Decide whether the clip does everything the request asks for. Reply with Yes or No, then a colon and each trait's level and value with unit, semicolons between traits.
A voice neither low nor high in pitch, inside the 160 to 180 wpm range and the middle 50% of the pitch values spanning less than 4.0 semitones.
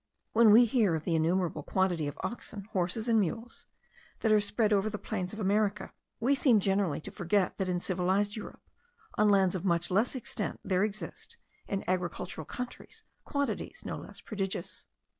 No: high, 200 Hz; average, 175 wpm; average, 3.0 semitones